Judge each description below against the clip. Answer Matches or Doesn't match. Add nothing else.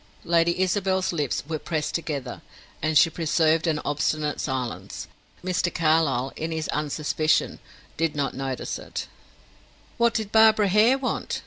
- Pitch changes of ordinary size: Matches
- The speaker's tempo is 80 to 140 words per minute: Matches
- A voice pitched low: Doesn't match